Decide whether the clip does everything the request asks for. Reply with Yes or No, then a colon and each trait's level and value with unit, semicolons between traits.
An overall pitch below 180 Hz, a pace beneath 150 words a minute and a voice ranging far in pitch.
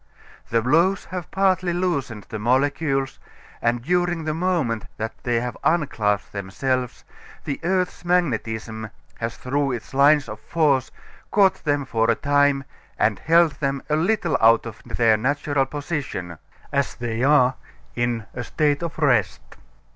Yes: medium, 140 Hz; average, 140 wpm; wide, 5.7 semitones